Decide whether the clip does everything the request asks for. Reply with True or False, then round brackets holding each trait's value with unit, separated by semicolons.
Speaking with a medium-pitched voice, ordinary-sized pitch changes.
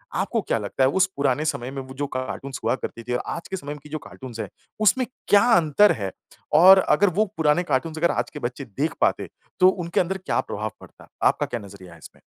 False (145 Hz; 6.1 semitones)